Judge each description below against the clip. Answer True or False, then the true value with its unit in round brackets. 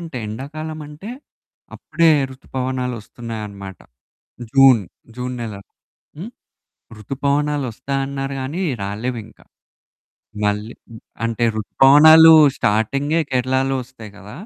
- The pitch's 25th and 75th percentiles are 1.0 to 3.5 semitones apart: False (4.2 semitones)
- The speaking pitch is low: True (130 Hz)